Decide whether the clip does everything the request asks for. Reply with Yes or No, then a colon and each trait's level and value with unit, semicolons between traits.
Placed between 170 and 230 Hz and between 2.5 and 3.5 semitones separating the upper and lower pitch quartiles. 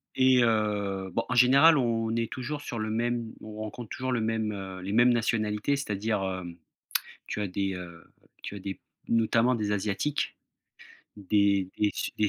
No: low, 110 Hz; average, 2.9 semitones